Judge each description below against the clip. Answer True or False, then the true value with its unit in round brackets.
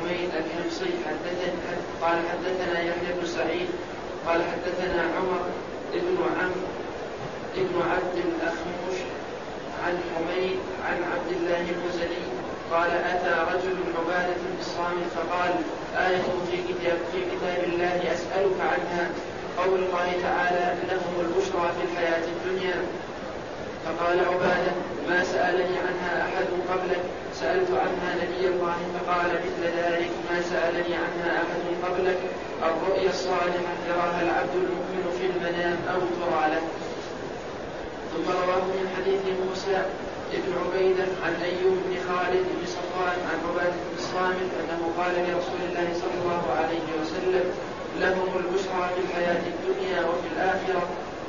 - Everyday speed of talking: True (120 wpm)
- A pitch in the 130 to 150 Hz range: False (175 Hz)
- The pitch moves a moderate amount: False (0.9 semitones)